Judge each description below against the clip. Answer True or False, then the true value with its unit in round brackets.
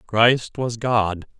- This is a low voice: True (115 Hz)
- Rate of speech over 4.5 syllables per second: False (2.6 syllables/s)